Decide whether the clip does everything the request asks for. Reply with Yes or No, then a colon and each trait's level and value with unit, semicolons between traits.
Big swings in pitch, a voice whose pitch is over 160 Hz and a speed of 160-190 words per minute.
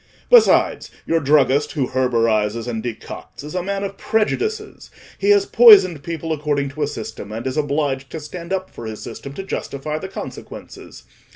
No: wide, 6.3 semitones; medium, 150 Hz; average, 175 wpm